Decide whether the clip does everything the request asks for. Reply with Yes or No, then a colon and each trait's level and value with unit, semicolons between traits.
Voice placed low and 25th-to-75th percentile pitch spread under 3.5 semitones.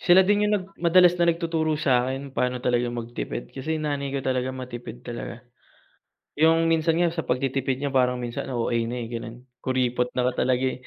No: low, 130 Hz; average, 4.7 semitones